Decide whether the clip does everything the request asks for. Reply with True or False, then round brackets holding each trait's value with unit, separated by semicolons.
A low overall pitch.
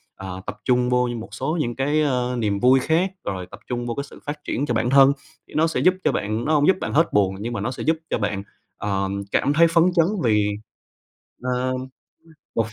True (125 Hz)